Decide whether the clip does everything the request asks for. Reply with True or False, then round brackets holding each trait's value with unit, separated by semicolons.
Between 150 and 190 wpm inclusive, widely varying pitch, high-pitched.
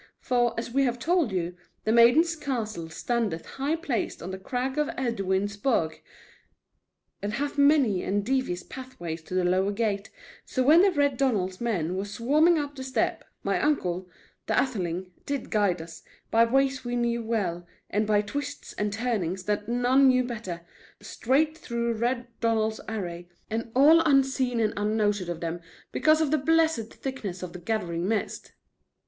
True (165 wpm; 5.8 semitones; 230 Hz)